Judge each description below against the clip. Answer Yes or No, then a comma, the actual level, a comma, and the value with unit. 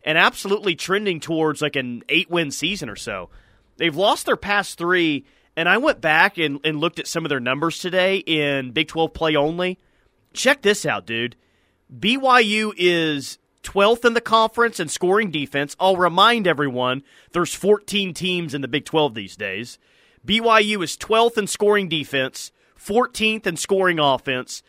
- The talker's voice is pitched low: No, medium, 170 Hz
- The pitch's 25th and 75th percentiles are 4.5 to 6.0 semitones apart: Yes, wide, 5.6 semitones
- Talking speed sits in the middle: Yes, average, 170 wpm